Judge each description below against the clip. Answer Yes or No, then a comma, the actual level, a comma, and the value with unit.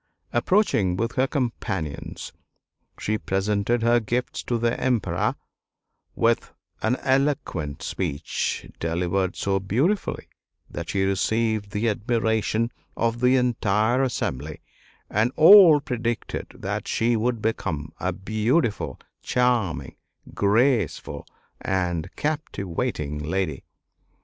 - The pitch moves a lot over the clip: No, average, 4.3 semitones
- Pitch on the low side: Yes, low, 110 Hz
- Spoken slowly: Yes, slow, 100 wpm